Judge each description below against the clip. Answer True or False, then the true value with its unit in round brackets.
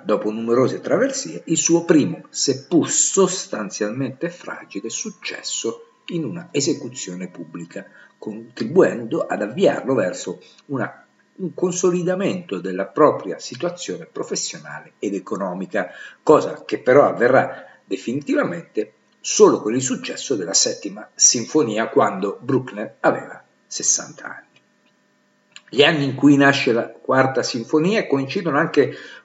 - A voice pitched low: False (160 Hz)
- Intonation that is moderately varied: False (6.8 semitones)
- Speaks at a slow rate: True (110 wpm)